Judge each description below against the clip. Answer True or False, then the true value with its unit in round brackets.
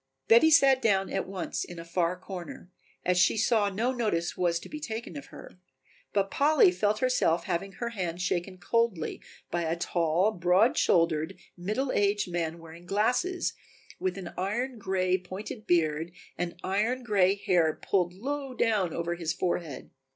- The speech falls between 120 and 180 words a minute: True (165 wpm)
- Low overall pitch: False (185 Hz)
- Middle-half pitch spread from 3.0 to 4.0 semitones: False (4.4 semitones)